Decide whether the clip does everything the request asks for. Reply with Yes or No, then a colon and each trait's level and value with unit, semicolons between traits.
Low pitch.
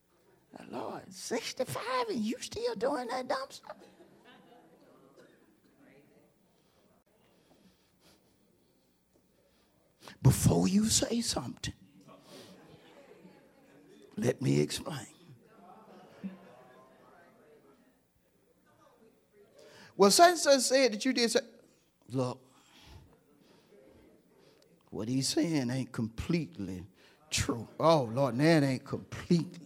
No: medium, 170 Hz